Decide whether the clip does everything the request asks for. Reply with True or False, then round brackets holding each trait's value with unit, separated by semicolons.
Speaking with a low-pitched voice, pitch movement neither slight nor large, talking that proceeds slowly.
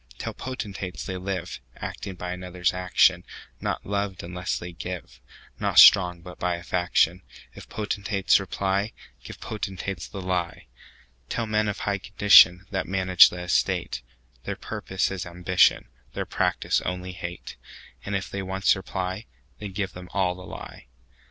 False (90 Hz; 1.7 semitones; 120 wpm)